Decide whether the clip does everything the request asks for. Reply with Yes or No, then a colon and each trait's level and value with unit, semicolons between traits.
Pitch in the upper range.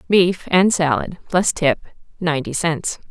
No: medium, 170 Hz